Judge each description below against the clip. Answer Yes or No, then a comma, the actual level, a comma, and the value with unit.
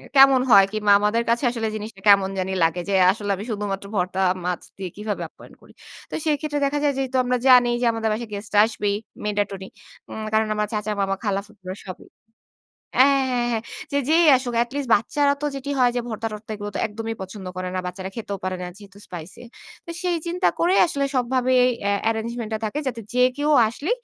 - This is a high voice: Yes, high, 220 Hz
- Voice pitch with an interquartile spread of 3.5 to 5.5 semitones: Yes, average, 4.1 semitones